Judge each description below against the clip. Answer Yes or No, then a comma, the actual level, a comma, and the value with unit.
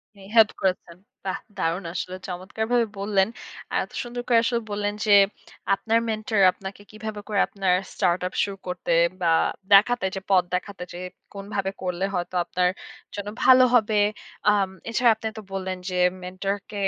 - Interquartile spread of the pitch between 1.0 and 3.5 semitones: Yes, average, 2.8 semitones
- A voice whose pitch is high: Yes, high, 200 Hz